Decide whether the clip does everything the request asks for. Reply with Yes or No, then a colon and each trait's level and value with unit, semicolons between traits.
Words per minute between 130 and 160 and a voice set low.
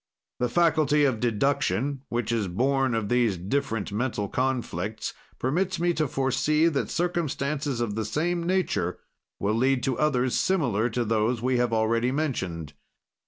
Yes: average, 150 wpm; low, 125 Hz